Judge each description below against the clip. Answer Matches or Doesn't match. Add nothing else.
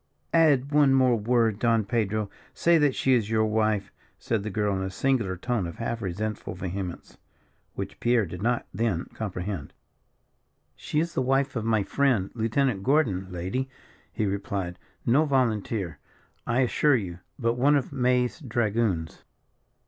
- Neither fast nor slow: Matches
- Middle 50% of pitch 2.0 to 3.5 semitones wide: Doesn't match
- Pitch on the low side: Matches